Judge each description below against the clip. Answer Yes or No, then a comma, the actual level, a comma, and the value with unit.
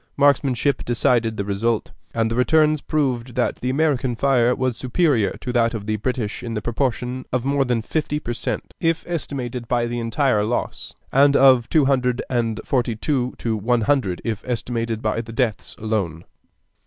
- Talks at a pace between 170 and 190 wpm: Yes, average, 180 wpm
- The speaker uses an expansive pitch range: No, average, 2.9 semitones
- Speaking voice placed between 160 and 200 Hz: No, low, 120 Hz